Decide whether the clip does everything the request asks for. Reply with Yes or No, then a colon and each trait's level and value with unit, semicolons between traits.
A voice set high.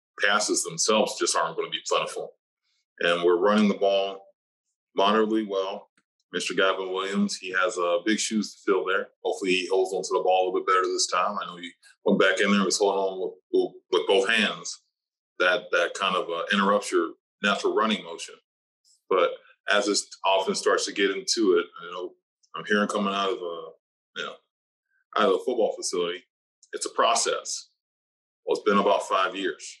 Yes: very high, 390 Hz